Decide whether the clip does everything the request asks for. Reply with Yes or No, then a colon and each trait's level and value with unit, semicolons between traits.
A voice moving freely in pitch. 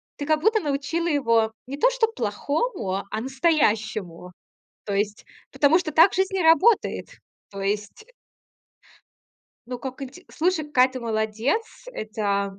Yes: wide, 7.3 semitones